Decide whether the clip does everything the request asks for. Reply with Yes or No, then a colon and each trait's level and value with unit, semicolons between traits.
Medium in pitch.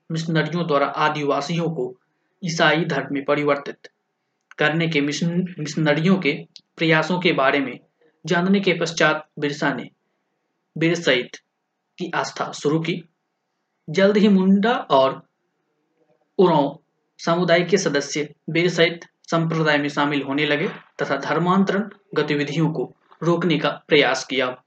Yes: medium, 160 Hz